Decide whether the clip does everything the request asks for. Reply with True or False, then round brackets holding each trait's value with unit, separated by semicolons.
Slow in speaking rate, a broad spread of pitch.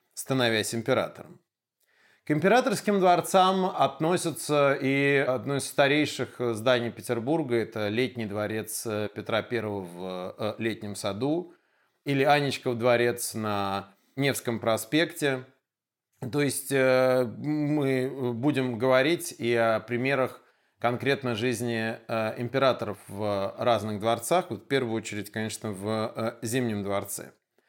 False (100 wpm; 4.0 semitones)